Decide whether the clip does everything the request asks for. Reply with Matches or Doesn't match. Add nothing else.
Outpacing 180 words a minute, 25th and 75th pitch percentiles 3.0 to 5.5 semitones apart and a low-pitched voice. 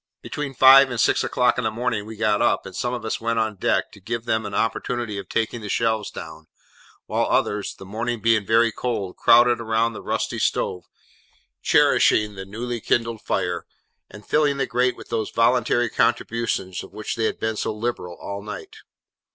Doesn't match